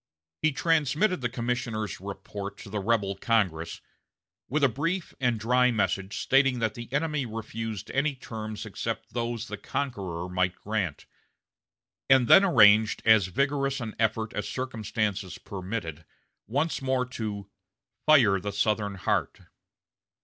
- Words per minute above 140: No, slow, 135 wpm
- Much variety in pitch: No, average, 4.5 semitones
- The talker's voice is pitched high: No, low, 115 Hz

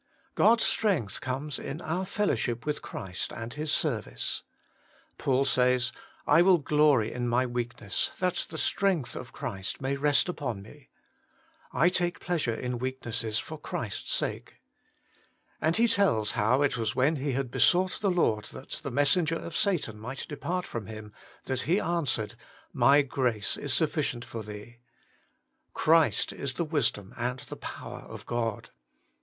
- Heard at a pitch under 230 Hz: Yes, low, 135 Hz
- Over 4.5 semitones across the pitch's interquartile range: Yes, wide, 5.4 semitones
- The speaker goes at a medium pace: Yes, average, 165 wpm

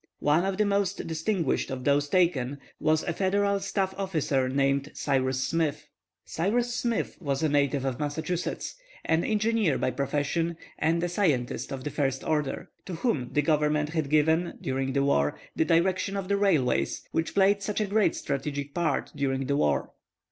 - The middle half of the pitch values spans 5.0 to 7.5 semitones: Yes, average, 5.3 semitones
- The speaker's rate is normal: Yes, average, 170 wpm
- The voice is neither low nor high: Yes, medium, 155 Hz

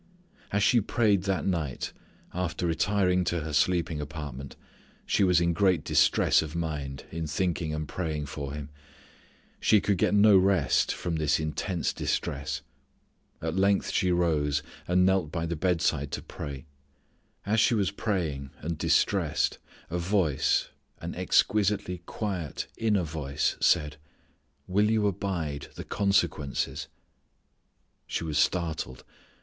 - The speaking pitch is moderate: No, very low, 85 Hz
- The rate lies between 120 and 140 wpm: Yes, slow, 135 wpm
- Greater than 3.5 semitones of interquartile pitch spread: Yes, average, 4.2 semitones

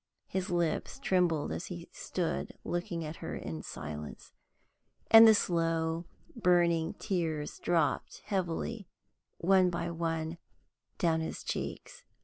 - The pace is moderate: No, slow, 120 wpm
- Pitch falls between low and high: Yes, medium, 170 Hz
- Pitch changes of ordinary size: No, narrow, 2.0 semitones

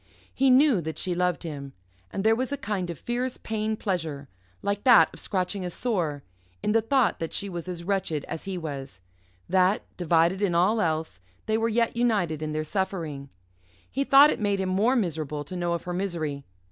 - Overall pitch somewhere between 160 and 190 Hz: Yes, medium, 185 Hz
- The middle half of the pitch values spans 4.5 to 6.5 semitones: Yes, average, 5.2 semitones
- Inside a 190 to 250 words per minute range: Yes, average, 200 wpm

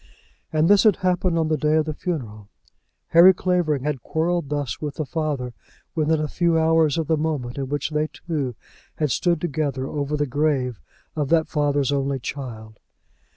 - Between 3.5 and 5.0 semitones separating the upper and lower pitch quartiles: No, average, 2.8 semitones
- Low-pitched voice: No, medium, 150 Hz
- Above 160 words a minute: Yes, average, 180 wpm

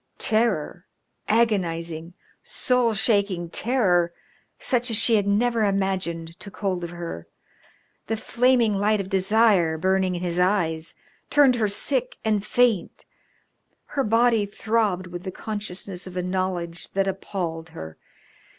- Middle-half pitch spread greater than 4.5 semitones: No, average, 4.0 semitones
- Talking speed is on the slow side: Yes, slow, 130 wpm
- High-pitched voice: Yes, high, 195 Hz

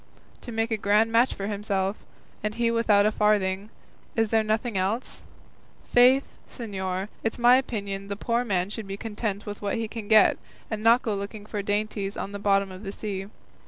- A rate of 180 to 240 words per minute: Yes, average, 195 wpm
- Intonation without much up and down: Yes, narrow, 2.2 semitones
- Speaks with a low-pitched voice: No, high, 210 Hz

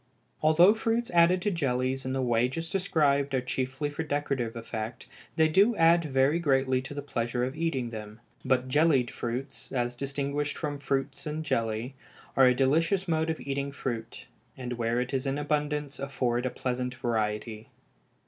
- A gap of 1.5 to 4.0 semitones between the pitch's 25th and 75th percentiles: Yes, average, 3.6 semitones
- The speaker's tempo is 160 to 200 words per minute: Yes, average, 170 wpm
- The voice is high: No, low, 135 Hz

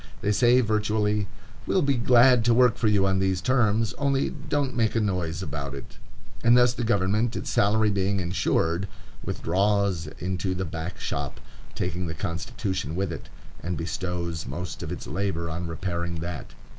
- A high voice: No, very low, 95 Hz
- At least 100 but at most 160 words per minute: No, average, 170 wpm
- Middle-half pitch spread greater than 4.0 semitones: Yes, average, 4.5 semitones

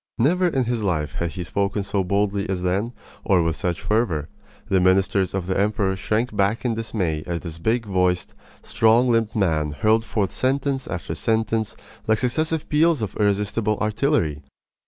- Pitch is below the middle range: Yes, low, 105 Hz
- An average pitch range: Yes, average, 3.8 semitones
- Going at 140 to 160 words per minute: No, average, 170 wpm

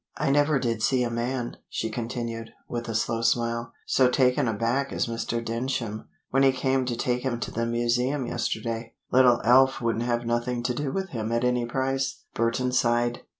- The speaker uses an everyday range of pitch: No, narrow, 1.9 semitones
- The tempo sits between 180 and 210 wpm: Yes, average, 190 wpm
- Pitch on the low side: Yes, low, 120 Hz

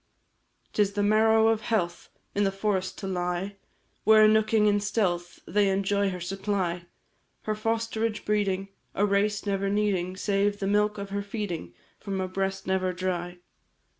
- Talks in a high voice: Yes, high, 200 Hz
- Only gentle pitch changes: Yes, narrow, 2.0 semitones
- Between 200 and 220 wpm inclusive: No, average, 155 wpm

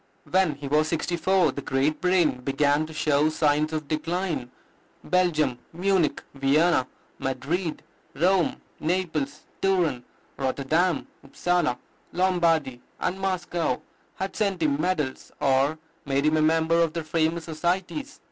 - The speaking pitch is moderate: Yes, medium, 160 Hz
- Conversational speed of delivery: No, slow, 130 wpm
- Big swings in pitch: No, average, 3.7 semitones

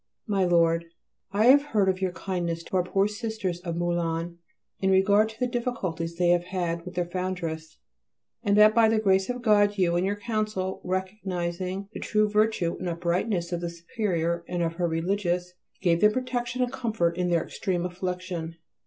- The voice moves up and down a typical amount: Yes, average, 3.5 semitones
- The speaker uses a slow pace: No, average, 185 wpm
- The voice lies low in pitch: No, medium, 185 Hz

